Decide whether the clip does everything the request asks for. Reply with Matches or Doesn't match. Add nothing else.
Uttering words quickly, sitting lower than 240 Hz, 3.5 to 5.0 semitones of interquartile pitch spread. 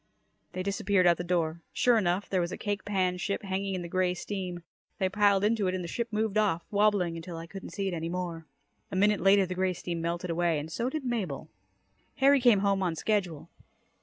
Doesn't match